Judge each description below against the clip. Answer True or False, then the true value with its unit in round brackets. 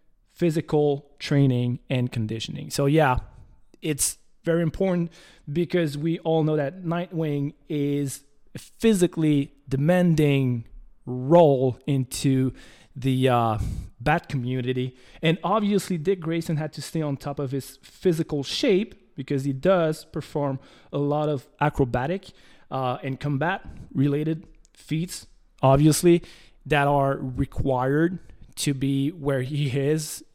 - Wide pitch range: False (3.5 semitones)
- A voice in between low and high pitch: True (145 Hz)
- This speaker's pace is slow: True (115 wpm)